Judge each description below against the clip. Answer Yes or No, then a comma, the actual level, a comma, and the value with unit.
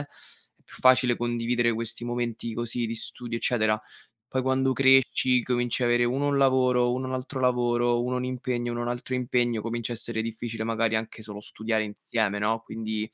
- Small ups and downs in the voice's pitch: Yes, narrow, 1.9 semitones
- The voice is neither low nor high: No, low, 120 Hz